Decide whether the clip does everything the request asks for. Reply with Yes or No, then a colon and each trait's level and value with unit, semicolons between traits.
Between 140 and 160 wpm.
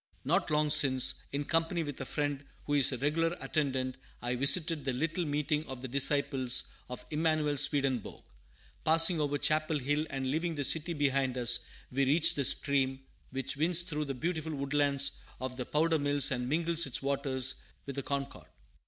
No: average, 175 wpm